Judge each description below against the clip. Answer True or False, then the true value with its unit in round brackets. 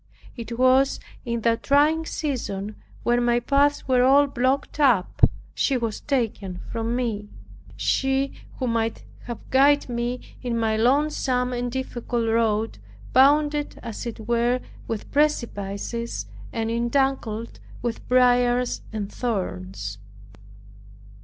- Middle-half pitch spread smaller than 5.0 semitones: True (2.9 semitones)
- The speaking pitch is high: True (240 Hz)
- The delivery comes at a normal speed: False (120 wpm)